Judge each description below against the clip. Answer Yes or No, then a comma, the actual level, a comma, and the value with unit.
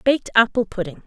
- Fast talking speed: No, average, 170 wpm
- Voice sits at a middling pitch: No, high, 215 Hz